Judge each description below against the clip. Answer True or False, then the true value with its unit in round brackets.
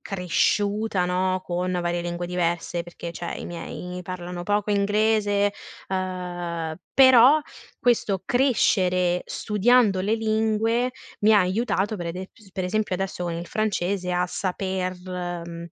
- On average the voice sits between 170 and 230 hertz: True (185 Hz)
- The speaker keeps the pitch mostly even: False (3.0 semitones)